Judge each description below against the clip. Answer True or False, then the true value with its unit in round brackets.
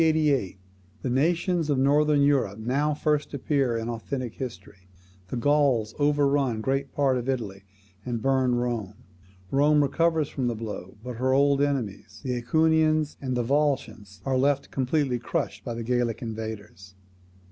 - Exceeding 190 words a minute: False (145 wpm)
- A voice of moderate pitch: False (130 Hz)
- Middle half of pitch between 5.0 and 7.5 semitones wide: False (3.9 semitones)